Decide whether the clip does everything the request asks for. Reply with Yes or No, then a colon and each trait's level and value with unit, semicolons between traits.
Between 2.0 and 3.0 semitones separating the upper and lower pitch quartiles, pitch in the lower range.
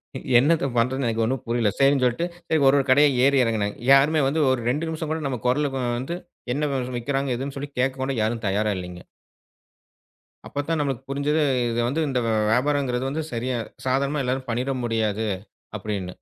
No: average, 3.4 semitones; low, 130 Hz